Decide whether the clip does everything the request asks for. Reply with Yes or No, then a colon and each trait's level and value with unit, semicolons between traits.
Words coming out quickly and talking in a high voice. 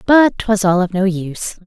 Yes: fast, 215 wpm; high, 200 Hz